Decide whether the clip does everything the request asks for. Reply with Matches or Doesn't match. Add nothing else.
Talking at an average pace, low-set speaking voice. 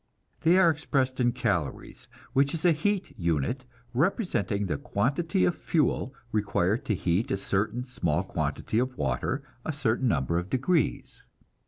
Matches